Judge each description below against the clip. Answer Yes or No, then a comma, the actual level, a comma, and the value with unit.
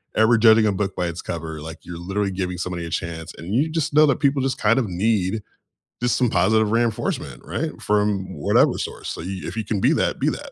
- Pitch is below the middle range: Yes, low, 105 Hz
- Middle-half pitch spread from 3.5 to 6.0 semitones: Yes, average, 4.3 semitones